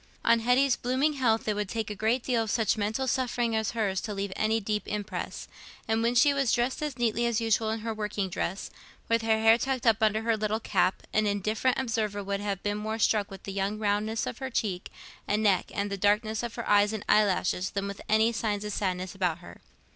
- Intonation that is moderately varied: No, narrow, 2.2 semitones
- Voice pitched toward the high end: Yes, high, 215 Hz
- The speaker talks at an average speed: No, fast, 230 wpm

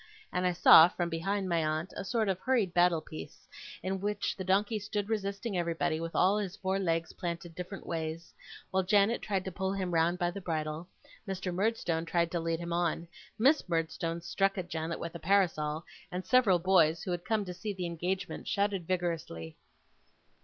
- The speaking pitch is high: No, medium, 180 Hz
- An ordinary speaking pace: Yes, average, 190 wpm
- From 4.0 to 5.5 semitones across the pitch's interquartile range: No, average, 2.8 semitones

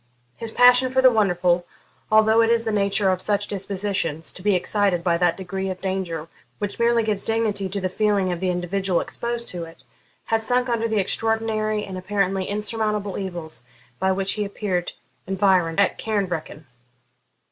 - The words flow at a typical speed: Yes, average, 170 wpm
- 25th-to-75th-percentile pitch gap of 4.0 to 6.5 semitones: No, average, 3.0 semitones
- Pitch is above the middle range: Yes, high, 200 Hz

